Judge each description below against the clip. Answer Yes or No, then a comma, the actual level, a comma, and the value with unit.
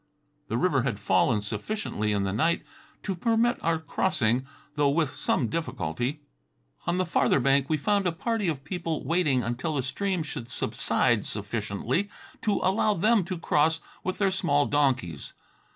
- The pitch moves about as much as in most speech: No, wide, 7.2 semitones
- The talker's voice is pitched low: No, medium, 150 Hz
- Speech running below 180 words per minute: Yes, average, 160 wpm